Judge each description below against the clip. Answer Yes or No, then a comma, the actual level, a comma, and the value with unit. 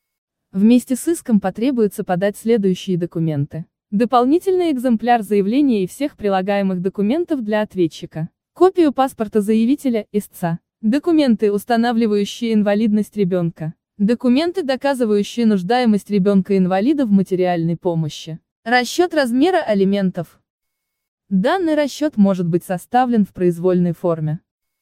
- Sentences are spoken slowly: Yes, slow, 105 wpm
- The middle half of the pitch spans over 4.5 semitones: Yes, average, 5.1 semitones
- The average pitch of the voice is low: No, high, 210 Hz